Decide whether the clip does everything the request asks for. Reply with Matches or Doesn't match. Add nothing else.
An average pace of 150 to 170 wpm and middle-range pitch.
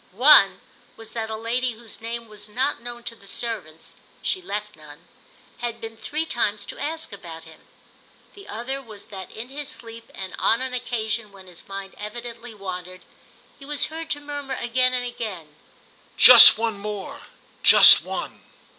Doesn't match